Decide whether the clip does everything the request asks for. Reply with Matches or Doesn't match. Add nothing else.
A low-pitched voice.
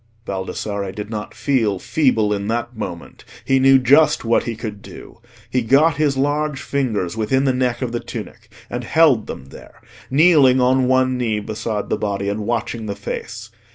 Matches